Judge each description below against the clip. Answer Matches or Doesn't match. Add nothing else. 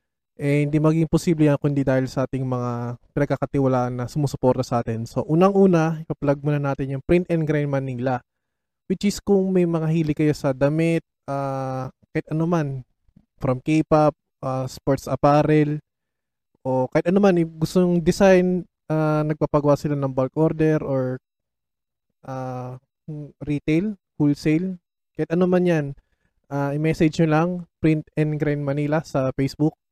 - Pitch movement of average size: Matches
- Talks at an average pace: Matches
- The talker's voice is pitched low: Doesn't match